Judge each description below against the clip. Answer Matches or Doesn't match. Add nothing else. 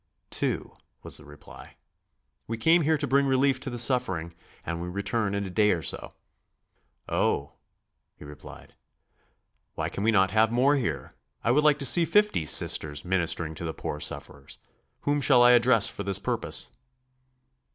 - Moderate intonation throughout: Doesn't match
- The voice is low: Matches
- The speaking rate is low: Doesn't match